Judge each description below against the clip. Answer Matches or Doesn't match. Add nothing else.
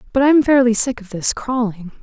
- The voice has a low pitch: Doesn't match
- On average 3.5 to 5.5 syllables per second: Doesn't match